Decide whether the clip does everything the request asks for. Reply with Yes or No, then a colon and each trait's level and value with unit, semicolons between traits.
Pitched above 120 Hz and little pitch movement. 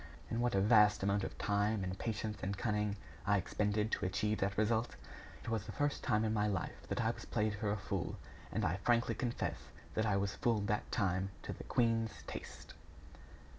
No: low, 105 Hz; narrow, 1.9 semitones